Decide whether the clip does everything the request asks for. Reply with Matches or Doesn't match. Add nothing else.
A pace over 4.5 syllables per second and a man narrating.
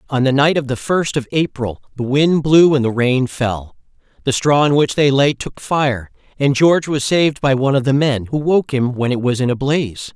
Matches